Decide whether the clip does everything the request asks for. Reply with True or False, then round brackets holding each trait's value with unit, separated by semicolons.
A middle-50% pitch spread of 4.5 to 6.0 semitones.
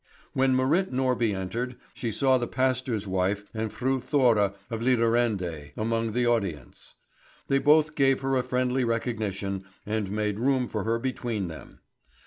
False (3.7 semitones)